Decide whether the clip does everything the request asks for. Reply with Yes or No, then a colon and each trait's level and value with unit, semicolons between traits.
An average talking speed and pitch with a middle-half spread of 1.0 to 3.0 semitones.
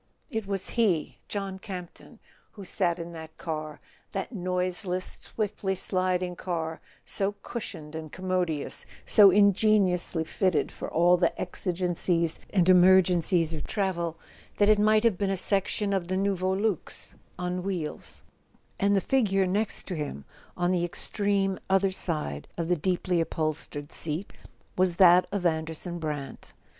Yes: average, 145 wpm; narrow, 2.6 semitones